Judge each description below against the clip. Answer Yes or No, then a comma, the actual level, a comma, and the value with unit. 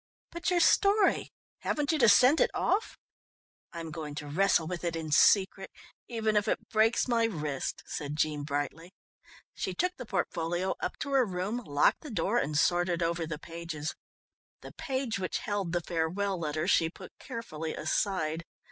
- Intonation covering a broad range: Yes, wide, 5.9 semitones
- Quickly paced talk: No, average, 170 wpm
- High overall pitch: No, medium, 180 Hz